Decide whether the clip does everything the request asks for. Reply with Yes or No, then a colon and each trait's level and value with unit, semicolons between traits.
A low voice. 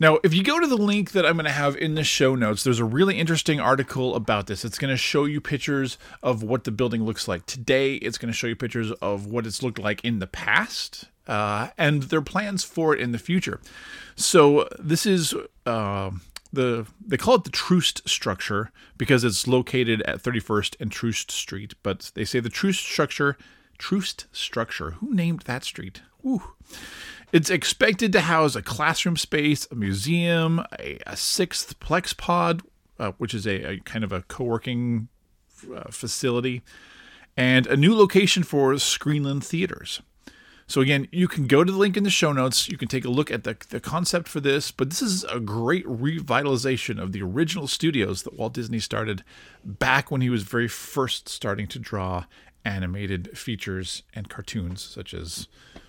Yes: low, 130 Hz